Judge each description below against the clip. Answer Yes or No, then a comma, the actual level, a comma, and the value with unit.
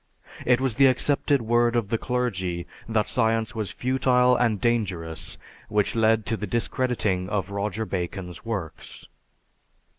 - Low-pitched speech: Yes, low, 110 Hz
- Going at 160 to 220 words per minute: No, average, 140 wpm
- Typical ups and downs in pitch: Yes, average, 3.9 semitones